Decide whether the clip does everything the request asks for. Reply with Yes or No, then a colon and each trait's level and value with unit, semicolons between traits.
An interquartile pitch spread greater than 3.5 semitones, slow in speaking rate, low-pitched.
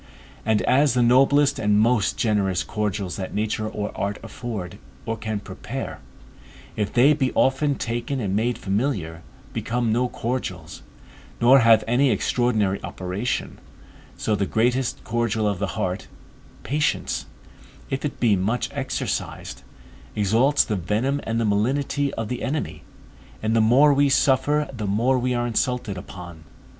No: average, 3.9 semitones; average, 145 wpm; low, 115 Hz